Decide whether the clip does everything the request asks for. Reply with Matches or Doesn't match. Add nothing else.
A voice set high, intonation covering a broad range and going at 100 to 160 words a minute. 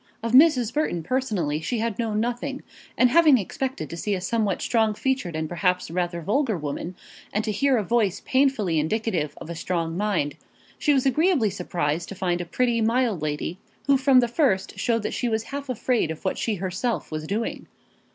Doesn't match